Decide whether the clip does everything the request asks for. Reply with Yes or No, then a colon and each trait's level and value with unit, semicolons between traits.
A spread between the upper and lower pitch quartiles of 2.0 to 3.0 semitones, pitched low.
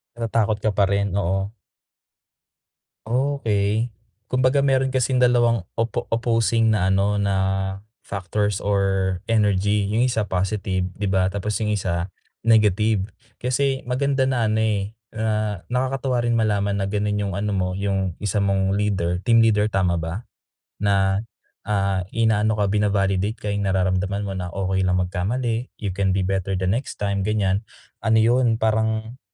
Yes: average, 2.7 semitones; low, 105 Hz